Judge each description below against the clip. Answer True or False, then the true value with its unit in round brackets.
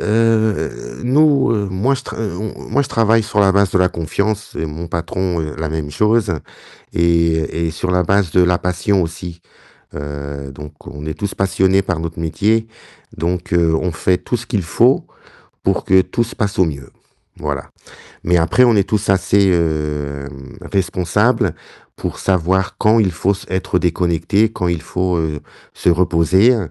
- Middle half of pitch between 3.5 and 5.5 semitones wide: True (4.0 semitones)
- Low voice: True (90 Hz)